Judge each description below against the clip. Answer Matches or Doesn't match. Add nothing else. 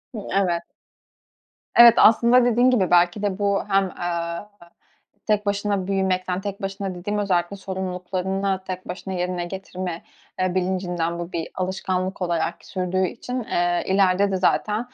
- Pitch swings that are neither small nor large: Doesn't match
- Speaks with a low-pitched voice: Doesn't match